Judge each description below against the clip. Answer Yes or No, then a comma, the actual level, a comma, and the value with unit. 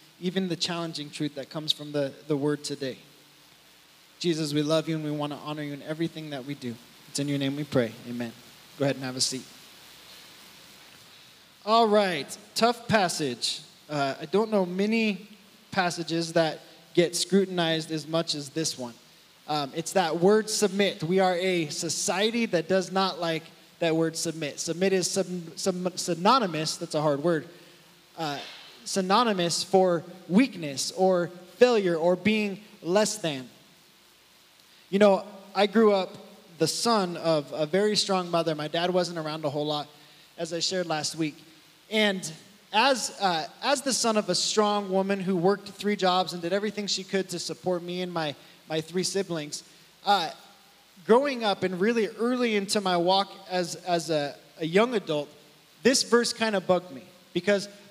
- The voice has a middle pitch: Yes, medium, 175 Hz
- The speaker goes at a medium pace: Yes, average, 170 wpm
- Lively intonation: No, average, 4.0 semitones